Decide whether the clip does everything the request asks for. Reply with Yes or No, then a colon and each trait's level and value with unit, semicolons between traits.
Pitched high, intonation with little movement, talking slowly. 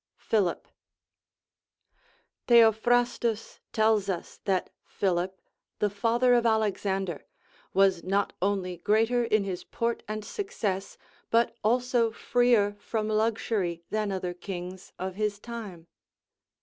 No: high, 210 Hz; average, 3.3 semitones; slow, 110 wpm